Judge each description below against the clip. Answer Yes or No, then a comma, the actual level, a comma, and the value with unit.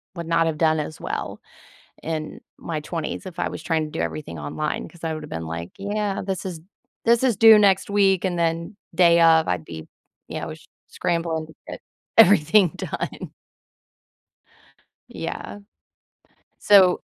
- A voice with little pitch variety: No, average, 3.7 semitones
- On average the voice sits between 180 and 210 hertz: No, medium, 165 Hz